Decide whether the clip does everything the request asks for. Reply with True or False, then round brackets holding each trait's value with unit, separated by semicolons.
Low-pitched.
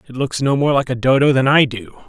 True (130 Hz)